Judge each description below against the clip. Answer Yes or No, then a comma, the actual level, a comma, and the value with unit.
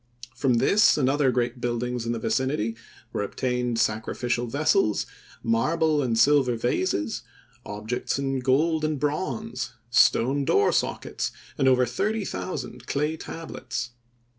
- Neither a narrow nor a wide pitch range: Yes, average, 3.9 semitones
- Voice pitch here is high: No, low, 130 Hz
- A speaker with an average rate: No, slow, 130 wpm